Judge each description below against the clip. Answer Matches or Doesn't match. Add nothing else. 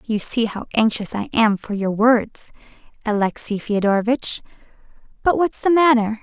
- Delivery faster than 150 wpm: Doesn't match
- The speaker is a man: Doesn't match